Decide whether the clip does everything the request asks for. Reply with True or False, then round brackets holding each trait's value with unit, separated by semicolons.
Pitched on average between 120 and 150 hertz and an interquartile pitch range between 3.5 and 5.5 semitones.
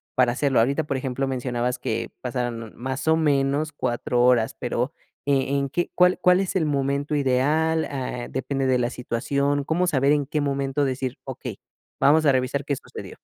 False (135 Hz; 2.6 semitones)